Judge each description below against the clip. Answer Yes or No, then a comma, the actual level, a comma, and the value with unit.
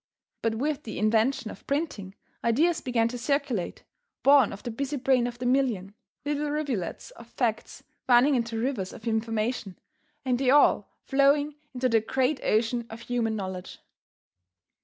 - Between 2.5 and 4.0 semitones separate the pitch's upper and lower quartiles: Yes, average, 3.7 semitones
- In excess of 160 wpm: No, average, 155 wpm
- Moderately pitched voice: No, high, 245 Hz